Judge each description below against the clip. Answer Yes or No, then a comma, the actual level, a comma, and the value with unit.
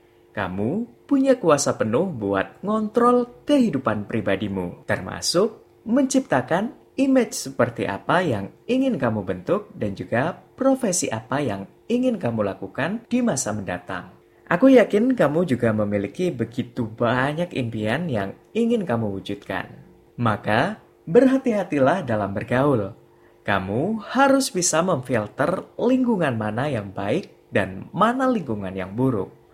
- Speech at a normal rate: Yes, average, 115 wpm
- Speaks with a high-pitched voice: No, low, 135 Hz